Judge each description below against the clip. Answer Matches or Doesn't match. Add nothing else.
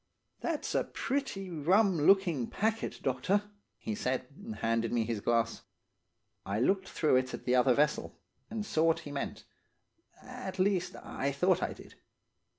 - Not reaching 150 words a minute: Doesn't match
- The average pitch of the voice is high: Doesn't match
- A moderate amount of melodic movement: Doesn't match